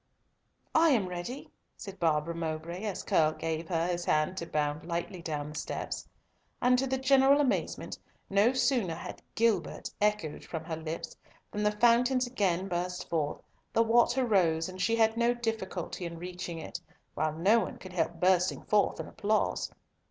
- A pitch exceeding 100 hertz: Yes, medium, 185 Hz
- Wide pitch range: Yes, wide, 5.7 semitones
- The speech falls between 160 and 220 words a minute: Yes, average, 170 wpm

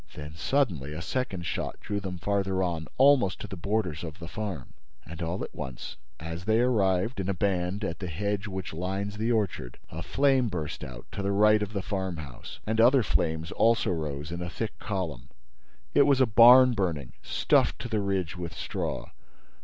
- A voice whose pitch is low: Yes, very low, 95 Hz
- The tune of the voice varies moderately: Yes, average, 4.5 semitones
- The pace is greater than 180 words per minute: Yes, average, 190 wpm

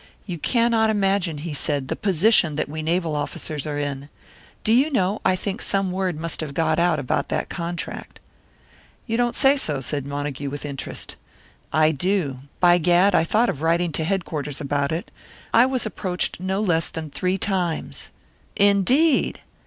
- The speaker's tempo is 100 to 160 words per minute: No, average, 170 wpm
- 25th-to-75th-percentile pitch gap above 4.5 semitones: Yes, average, 5.0 semitones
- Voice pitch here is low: No, medium, 175 Hz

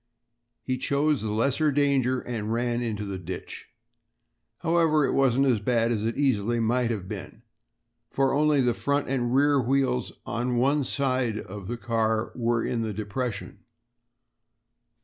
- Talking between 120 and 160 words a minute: Yes, average, 150 wpm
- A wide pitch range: No, average, 3.4 semitones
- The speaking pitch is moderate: No, low, 120 Hz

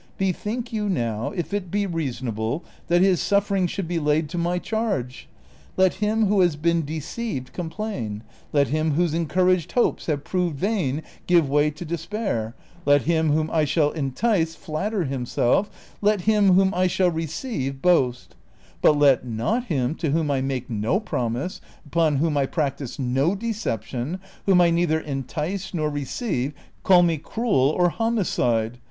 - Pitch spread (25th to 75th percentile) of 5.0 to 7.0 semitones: Yes, wide, 5.5 semitones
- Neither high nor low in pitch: Yes, medium, 165 Hz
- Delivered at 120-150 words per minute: No, average, 160 wpm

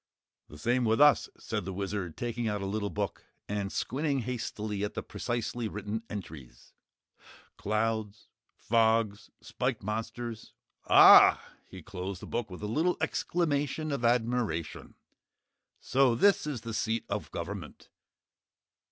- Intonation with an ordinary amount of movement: Yes, average, 3.3 semitones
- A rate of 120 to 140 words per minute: Yes, slow, 135 wpm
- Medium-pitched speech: No, low, 110 Hz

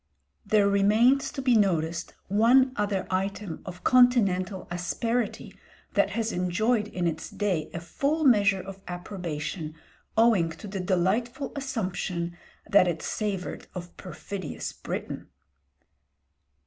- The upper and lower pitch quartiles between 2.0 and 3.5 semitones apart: No, average, 4.3 semitones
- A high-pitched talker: Yes, high, 195 Hz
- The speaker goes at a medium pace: No, slow, 120 wpm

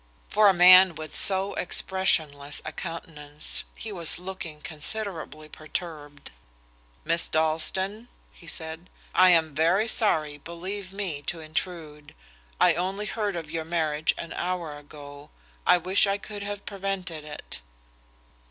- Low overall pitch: No, medium, 170 Hz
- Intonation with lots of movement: No, average, 3.7 semitones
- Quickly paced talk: No, slow, 135 wpm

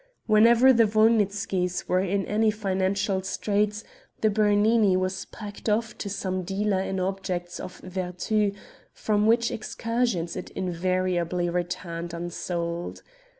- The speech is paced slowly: Yes, slow, 120 wpm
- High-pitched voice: Yes, high, 195 Hz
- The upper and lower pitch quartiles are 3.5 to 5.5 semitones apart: No, average, 2.8 semitones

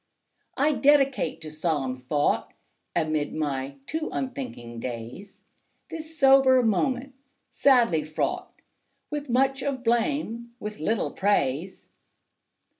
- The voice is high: Yes, high, 225 Hz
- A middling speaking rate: No, slow, 105 wpm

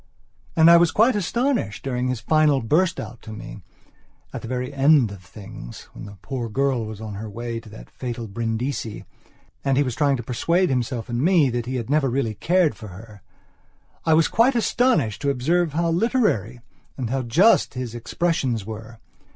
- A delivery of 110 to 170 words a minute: No, average, 185 wpm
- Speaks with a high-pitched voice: No, low, 125 Hz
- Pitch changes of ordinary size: No, wide, 6.0 semitones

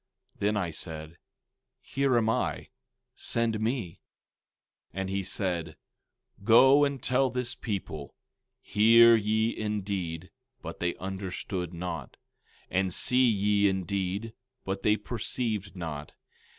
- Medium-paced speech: No, slow, 110 wpm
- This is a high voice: No, low, 100 Hz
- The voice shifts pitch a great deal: No, average, 4.0 semitones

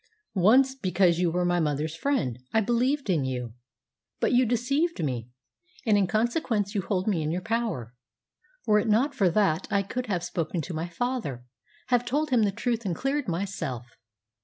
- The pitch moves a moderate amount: No, wide, 6.5 semitones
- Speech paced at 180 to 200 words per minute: Yes, average, 185 wpm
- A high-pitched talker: Yes, high, 200 Hz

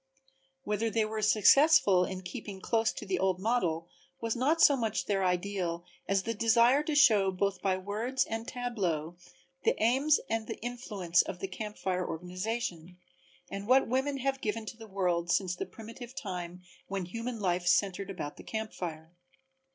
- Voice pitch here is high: Yes, high, 205 Hz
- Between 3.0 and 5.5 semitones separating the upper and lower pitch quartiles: Yes, average, 4.2 semitones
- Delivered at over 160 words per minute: Yes, average, 175 wpm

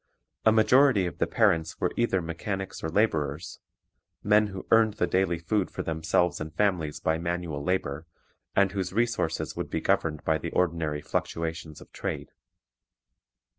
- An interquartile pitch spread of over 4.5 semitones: No, average, 4.2 semitones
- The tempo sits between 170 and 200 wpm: No, average, 155 wpm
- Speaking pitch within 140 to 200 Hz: No, very low, 90 Hz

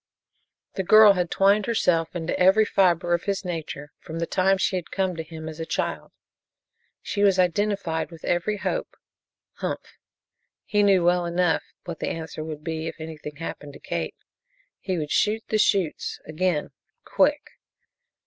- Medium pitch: Yes, medium, 175 Hz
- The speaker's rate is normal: Yes, average, 165 wpm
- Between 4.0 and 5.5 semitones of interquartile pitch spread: No, average, 3.3 semitones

